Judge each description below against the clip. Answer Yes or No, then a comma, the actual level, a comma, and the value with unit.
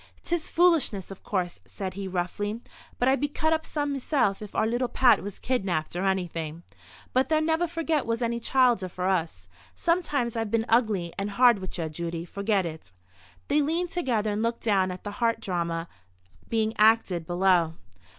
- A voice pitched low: No, high, 210 Hz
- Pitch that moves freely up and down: Yes, wide, 5.7 semitones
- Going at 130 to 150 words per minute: No, average, 180 wpm